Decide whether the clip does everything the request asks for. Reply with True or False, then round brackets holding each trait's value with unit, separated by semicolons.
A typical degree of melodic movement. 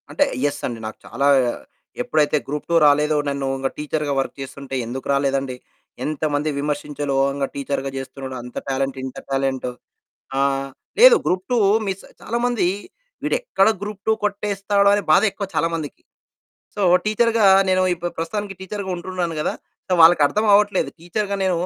False (6.4 semitones)